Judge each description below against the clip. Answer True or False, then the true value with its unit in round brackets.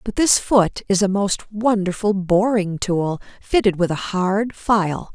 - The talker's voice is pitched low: False (200 Hz)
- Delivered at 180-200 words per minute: False (165 wpm)